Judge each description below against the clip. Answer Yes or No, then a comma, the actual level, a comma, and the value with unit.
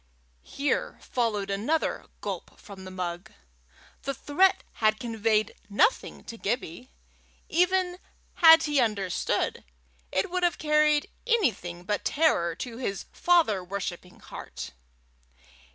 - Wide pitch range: Yes, wide, 8.2 semitones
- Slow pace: Yes, slow, 115 wpm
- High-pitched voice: Yes, high, 230 Hz